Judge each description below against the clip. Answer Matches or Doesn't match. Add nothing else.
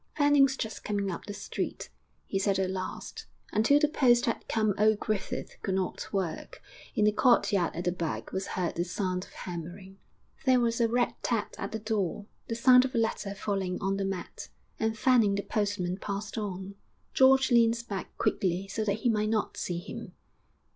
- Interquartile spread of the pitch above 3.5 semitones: Doesn't match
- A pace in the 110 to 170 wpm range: Doesn't match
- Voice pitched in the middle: Doesn't match